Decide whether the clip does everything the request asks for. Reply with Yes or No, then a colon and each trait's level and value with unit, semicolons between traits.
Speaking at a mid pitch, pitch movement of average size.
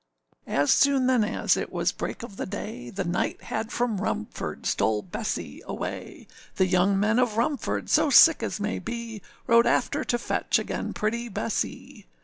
No: high, 220 Hz; average, 3.5 semitones